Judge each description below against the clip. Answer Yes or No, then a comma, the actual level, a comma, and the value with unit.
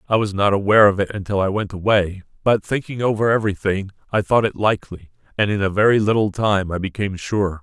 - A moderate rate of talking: No, fast, 210 wpm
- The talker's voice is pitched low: Yes, low, 100 Hz